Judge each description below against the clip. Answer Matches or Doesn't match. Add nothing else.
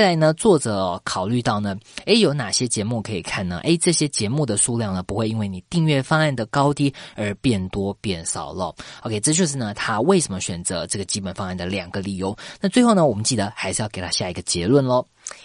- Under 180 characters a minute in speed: Doesn't match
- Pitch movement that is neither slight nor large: Doesn't match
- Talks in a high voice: Doesn't match